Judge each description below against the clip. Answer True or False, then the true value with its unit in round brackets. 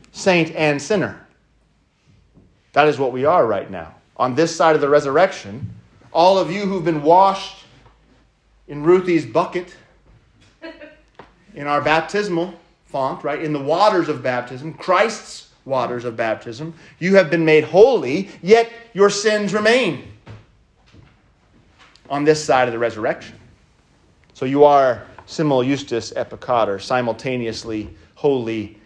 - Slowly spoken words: True (130 wpm)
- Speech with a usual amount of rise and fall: False (6.2 semitones)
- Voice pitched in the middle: True (155 Hz)